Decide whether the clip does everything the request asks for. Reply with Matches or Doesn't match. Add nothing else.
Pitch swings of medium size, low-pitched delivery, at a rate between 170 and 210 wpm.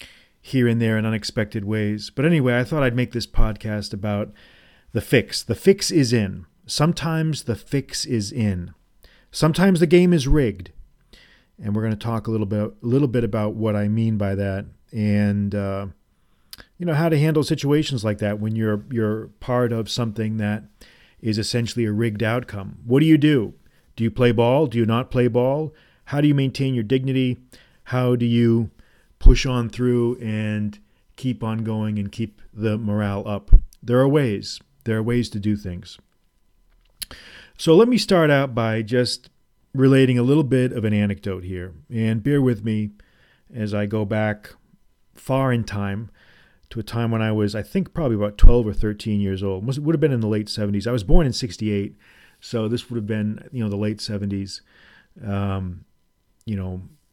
Matches